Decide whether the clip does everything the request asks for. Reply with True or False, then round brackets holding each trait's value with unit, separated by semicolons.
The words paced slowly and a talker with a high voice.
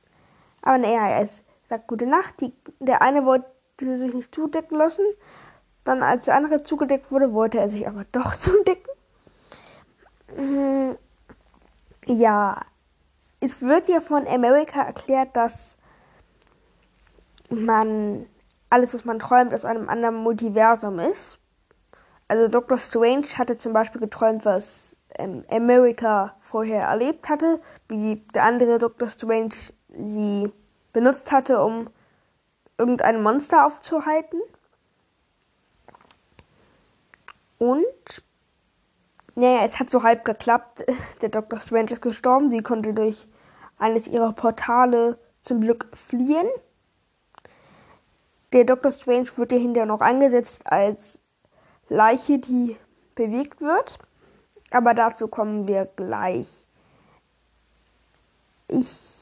True (110 wpm; 240 Hz)